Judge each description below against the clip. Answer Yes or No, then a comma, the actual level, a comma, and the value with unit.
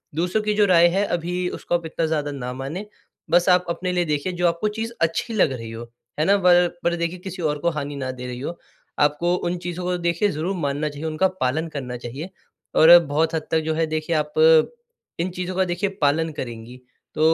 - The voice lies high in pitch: No, medium, 165 Hz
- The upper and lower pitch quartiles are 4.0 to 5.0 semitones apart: No, average, 3.4 semitones